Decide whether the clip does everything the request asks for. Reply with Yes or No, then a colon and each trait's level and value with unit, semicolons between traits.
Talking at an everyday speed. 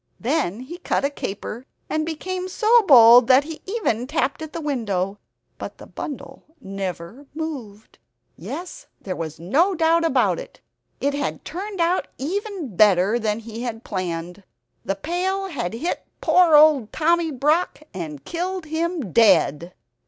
Yes: average, 150 wpm